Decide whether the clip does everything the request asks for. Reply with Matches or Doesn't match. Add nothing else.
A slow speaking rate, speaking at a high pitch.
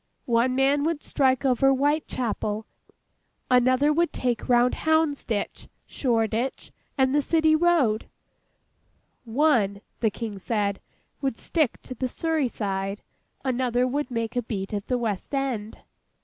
Matches